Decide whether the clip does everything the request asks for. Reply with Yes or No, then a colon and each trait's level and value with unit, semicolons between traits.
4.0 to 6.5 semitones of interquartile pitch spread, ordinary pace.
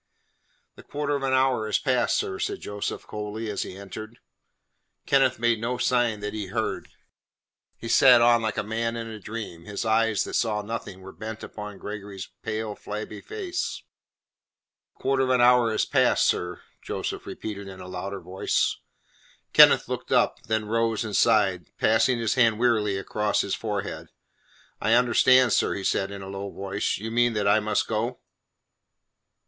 No: average, 2.7 semitones; average, 175 wpm